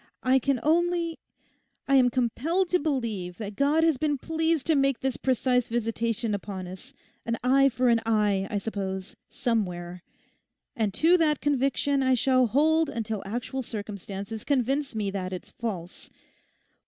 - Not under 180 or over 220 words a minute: No, average, 145 wpm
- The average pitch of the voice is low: No, high, 245 Hz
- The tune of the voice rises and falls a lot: No, average, 5.0 semitones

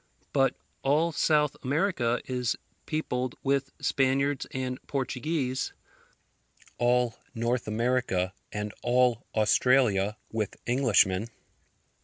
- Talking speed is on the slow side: Yes, slow, 90 wpm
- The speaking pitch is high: No, low, 125 Hz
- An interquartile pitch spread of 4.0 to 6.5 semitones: No, average, 2.8 semitones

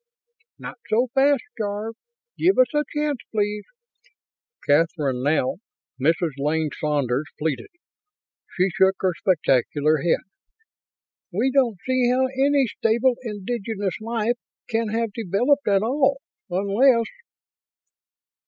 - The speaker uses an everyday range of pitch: No, wide, 6.9 semitones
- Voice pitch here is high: Yes, high, 215 Hz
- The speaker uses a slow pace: Yes, slow, 110 wpm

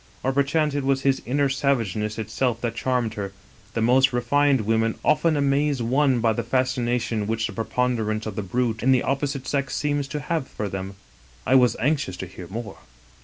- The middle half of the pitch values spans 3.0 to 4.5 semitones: Yes, average, 3.7 semitones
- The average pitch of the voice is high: No, low, 125 Hz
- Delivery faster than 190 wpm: Yes, average, 200 wpm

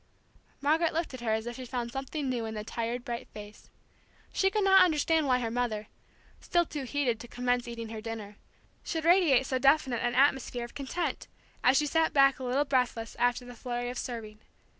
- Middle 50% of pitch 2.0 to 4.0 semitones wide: Yes, average, 3.4 semitones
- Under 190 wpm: No, fast, 205 wpm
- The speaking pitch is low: No, very high, 250 Hz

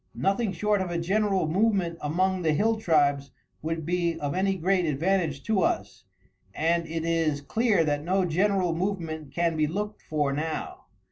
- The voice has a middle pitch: Yes, medium, 170 Hz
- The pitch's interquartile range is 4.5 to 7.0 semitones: No, average, 3.6 semitones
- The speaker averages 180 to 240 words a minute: No, average, 165 wpm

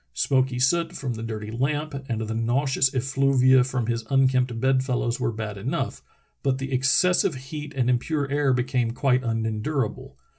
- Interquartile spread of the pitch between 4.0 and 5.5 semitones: No, narrow, 2.6 semitones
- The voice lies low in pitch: Yes, low, 130 Hz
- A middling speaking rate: Yes, average, 160 wpm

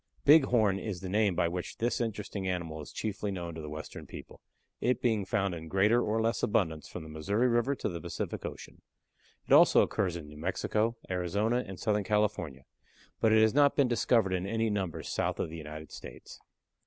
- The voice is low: Yes, low, 100 Hz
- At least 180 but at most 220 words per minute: Yes, average, 195 wpm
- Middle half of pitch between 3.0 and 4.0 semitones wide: No, average, 4.6 semitones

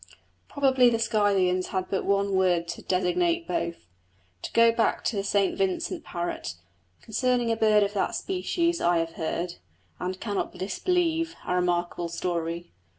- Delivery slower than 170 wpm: Yes, average, 155 wpm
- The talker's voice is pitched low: No, high, 200 Hz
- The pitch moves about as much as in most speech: Yes, average, 5.0 semitones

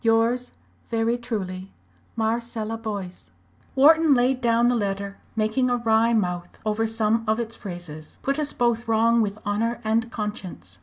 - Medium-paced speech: Yes, average, 150 wpm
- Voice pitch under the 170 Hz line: No, high, 225 Hz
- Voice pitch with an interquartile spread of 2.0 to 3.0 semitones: Yes, narrow, 2.5 semitones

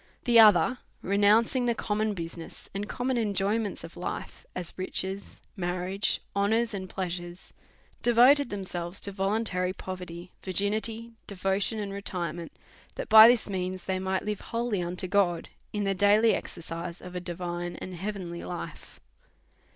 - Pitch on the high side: Yes, high, 195 Hz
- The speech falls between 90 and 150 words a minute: Yes, average, 145 wpm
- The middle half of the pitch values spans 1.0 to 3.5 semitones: Yes, average, 3.1 semitones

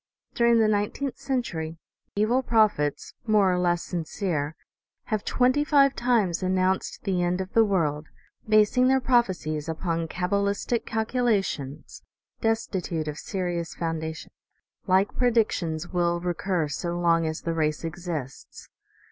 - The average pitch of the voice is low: No, medium, 185 Hz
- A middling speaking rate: No, slow, 130 wpm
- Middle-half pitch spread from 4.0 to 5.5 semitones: Yes, average, 5.0 semitones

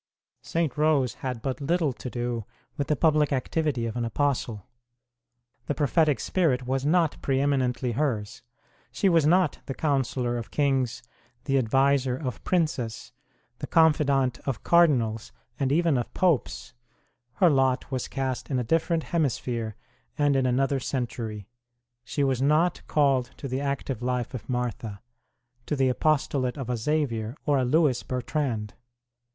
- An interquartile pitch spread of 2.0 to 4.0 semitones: Yes, average, 3.4 semitones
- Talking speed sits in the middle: Yes, average, 150 wpm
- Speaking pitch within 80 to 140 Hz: Yes, low, 135 Hz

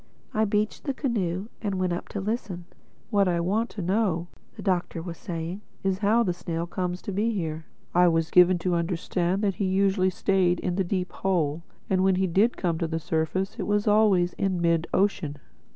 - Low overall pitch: No, medium, 185 Hz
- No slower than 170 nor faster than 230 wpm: Yes, fast, 205 wpm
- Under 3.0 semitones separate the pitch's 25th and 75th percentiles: Yes, narrow, 2.6 semitones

